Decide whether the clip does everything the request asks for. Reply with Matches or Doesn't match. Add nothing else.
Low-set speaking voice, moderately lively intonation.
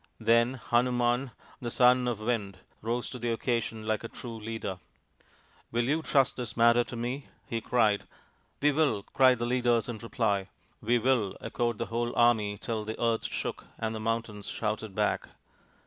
Doesn't match